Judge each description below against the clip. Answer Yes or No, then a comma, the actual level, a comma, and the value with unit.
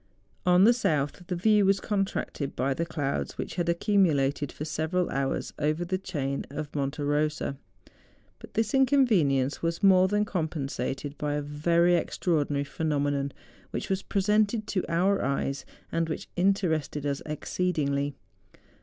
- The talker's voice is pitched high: No, medium, 160 Hz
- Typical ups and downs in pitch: Yes, average, 4.7 semitones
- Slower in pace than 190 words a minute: Yes, average, 145 wpm